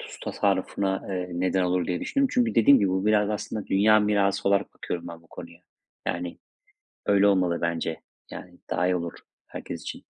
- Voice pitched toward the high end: No, very low, 95 Hz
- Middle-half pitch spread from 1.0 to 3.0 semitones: Yes, narrow, 2.6 semitones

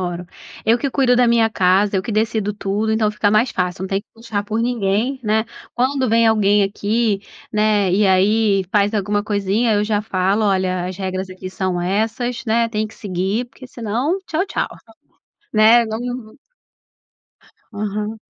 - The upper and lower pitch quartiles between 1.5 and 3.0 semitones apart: Yes, narrow, 2.6 semitones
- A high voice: Yes, high, 210 Hz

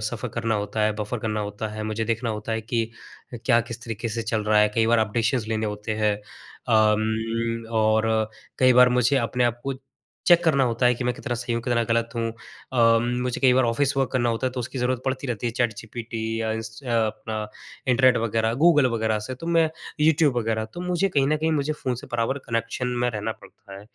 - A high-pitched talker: No, low, 115 Hz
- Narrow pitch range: Yes, narrow, 2.3 semitones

